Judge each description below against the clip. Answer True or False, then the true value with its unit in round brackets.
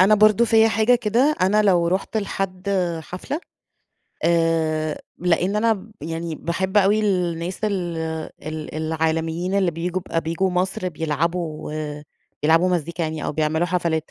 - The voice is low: False (175 Hz)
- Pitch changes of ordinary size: True (3.5 semitones)